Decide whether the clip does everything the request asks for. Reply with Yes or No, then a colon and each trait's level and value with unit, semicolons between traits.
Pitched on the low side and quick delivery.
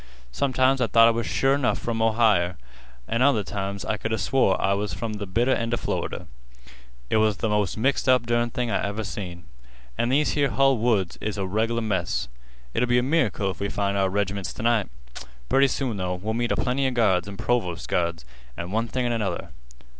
Yes: low, 110 Hz; fast, 215 wpm